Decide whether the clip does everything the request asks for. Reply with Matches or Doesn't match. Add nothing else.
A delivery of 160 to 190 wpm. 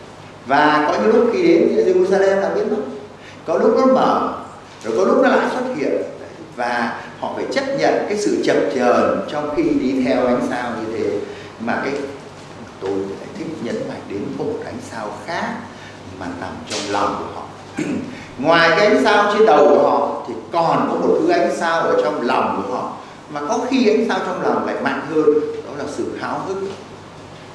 Doesn't match